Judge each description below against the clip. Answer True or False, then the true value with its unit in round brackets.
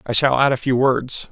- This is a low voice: True (130 Hz)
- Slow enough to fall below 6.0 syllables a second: True (5.0 syllables/s)